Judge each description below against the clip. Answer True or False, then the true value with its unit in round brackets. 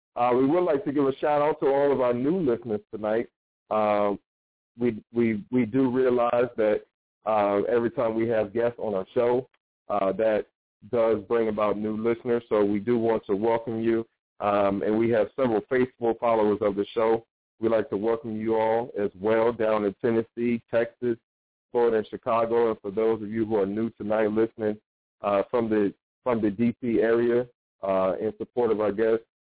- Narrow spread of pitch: True (1.9 semitones)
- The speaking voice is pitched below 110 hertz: False (115 Hz)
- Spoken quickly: False (190 wpm)